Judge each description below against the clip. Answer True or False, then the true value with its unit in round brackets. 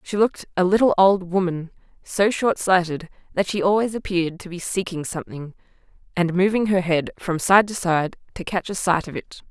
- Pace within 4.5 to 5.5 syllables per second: True (5.3 syllables/s)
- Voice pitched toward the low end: False (185 Hz)